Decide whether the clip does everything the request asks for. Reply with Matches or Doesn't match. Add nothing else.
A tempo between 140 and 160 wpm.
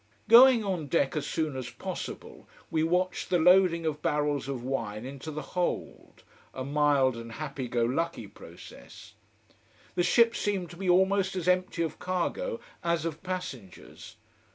Matches